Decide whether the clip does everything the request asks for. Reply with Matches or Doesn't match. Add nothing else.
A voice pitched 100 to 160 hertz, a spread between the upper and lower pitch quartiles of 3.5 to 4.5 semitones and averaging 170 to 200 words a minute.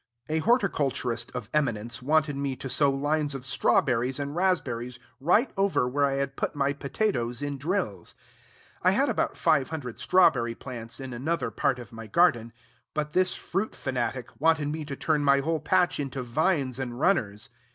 Matches